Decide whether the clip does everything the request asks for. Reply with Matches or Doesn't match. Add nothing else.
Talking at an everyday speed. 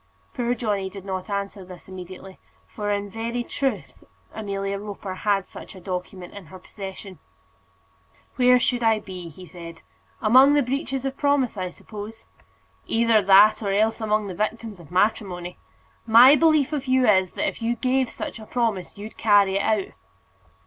Matches